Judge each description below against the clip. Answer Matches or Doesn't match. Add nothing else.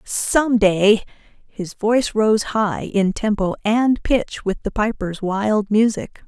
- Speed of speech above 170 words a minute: Doesn't match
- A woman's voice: Matches